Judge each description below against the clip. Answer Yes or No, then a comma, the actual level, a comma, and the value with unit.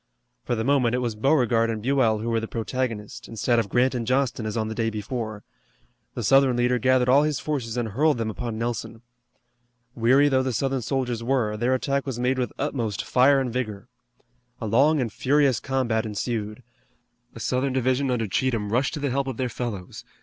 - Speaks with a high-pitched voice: No, low, 125 Hz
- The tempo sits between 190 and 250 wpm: Yes, average, 200 wpm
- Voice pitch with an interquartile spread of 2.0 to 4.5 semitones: Yes, average, 2.8 semitones